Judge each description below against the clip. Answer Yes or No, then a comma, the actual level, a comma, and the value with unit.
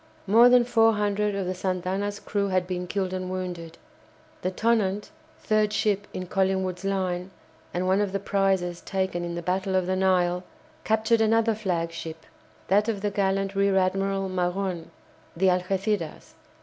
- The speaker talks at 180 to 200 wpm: No, average, 160 wpm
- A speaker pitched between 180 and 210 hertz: Yes, high, 190 Hz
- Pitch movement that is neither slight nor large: No, narrow, 1.9 semitones